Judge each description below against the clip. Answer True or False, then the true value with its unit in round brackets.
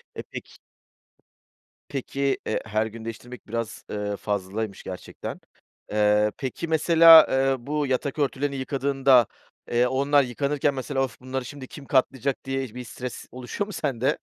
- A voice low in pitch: True (130 Hz)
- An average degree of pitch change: True (3.3 semitones)